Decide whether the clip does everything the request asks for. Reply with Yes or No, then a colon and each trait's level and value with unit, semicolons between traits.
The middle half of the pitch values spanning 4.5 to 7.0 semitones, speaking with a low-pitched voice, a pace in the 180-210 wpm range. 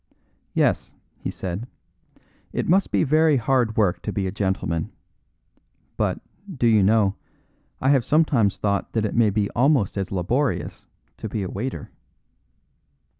No: average, 5.1 semitones; low, 110 Hz; average, 145 wpm